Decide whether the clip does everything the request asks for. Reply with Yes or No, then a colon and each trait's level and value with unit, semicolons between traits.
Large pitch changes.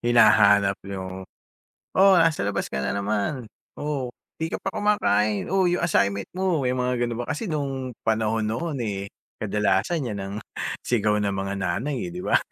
Yes: wide, 6.8 semitones